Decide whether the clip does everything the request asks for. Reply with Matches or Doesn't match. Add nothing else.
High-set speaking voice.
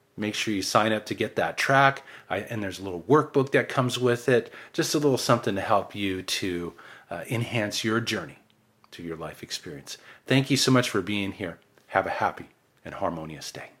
Doesn't match